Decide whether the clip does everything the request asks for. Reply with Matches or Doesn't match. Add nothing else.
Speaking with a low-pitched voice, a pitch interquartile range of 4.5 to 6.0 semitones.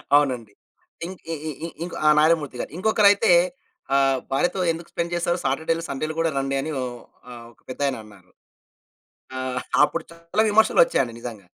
Doesn't match